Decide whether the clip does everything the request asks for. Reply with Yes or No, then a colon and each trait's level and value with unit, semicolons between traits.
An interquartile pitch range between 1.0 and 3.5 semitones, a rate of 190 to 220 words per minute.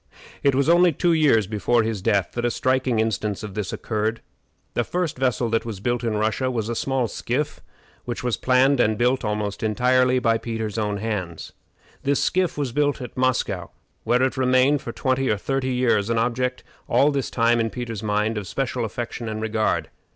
Yes: average, 3.0 semitones; average, 195 wpm